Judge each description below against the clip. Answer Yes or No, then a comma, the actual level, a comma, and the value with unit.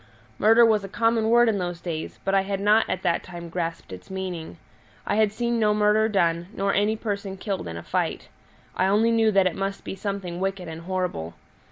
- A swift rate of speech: Yes, fast, 215 wpm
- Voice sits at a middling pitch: No, high, 195 Hz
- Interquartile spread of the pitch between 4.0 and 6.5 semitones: No, average, 3.3 semitones